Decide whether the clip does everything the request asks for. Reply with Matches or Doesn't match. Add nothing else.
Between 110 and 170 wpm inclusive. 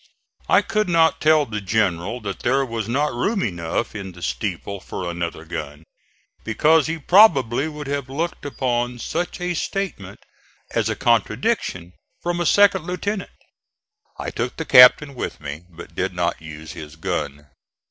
Matches